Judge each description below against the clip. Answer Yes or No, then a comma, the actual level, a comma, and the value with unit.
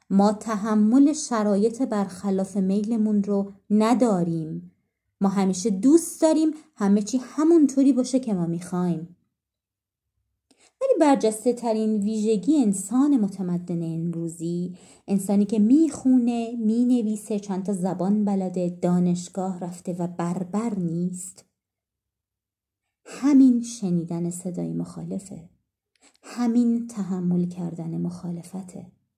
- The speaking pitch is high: Yes, high, 200 Hz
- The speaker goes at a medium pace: No, slow, 95 wpm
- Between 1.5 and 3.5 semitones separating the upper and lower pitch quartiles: No, average, 4.8 semitones